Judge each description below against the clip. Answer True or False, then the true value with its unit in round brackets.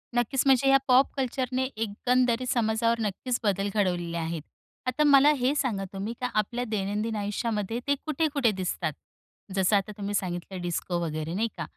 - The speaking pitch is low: False (220 Hz)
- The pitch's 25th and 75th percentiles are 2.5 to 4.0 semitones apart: False (4.7 semitones)